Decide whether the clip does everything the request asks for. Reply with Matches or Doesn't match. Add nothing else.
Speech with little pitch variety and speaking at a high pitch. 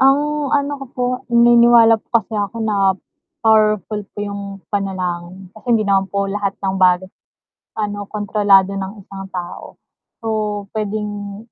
Matches